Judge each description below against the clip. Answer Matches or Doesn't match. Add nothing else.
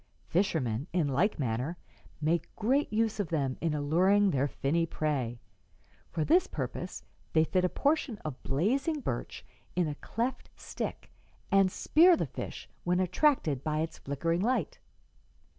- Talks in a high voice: Doesn't match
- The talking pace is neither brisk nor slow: Matches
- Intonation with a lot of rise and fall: Matches